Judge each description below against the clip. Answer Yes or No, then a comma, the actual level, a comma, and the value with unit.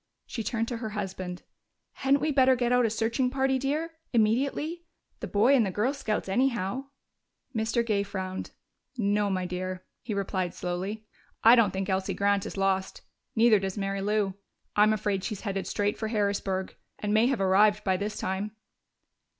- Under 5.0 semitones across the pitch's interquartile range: Yes, average, 3.6 semitones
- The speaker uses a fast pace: No, average, 175 wpm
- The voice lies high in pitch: Yes, high, 210 Hz